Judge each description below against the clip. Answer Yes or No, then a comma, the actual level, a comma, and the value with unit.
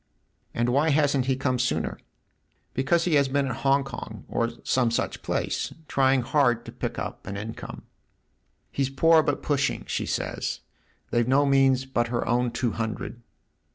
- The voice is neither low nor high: No, low, 130 Hz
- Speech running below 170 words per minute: No, average, 180 wpm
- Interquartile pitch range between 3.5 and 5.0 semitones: No, average, 2.7 semitones